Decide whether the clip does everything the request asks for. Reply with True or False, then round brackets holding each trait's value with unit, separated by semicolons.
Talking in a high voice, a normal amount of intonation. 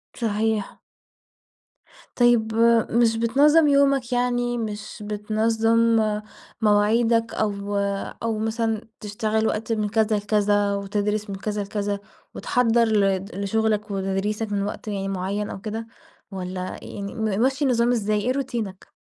False (215 Hz; 2.0 semitones)